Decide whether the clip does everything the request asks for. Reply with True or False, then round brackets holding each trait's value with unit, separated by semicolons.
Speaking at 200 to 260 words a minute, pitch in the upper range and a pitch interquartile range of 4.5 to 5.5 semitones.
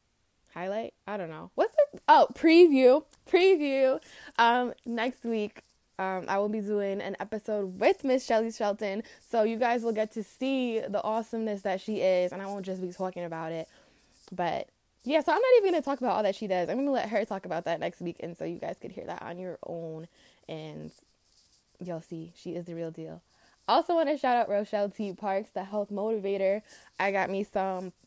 True (205 wpm; 205 Hz; 4.8 semitones)